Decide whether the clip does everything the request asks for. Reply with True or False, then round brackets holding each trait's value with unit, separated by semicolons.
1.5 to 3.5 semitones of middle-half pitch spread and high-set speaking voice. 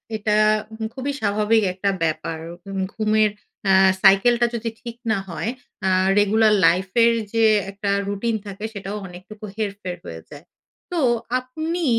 True (2.9 semitones; 210 Hz)